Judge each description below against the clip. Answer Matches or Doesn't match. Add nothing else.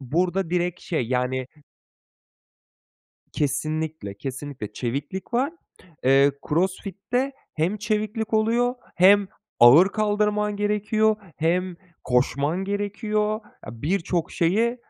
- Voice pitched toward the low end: Doesn't match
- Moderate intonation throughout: Doesn't match